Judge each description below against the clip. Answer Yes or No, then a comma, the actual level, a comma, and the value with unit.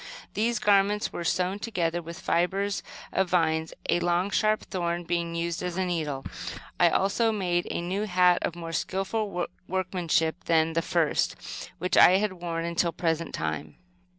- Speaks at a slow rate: No, average, 165 wpm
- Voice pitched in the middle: Yes, medium, 175 Hz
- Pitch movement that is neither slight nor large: No, narrow, 2.3 semitones